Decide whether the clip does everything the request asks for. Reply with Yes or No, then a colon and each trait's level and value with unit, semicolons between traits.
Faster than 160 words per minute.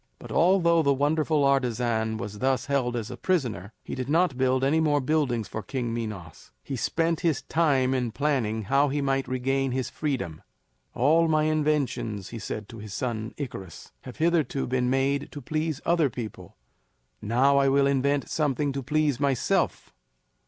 Yes: average, 170 wpm